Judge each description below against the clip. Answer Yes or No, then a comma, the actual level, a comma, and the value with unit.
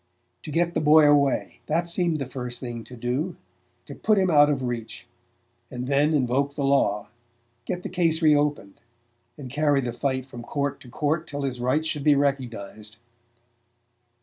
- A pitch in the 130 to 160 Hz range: Yes, medium, 140 Hz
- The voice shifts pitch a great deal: No, average, 3.6 semitones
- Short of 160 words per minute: No, average, 175 wpm